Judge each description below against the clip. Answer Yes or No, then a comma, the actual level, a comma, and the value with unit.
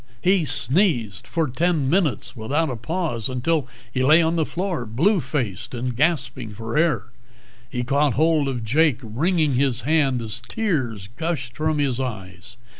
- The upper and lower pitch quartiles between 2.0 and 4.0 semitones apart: No, average, 5.2 semitones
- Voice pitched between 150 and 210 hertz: No, low, 135 Hz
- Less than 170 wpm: Yes, average, 160 wpm